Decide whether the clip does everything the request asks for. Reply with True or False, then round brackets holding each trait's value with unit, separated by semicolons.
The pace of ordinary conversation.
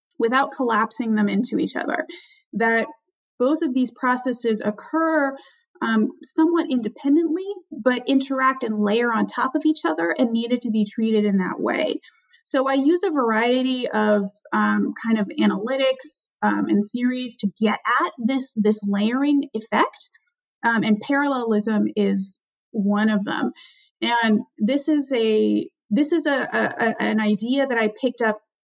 True (155 wpm)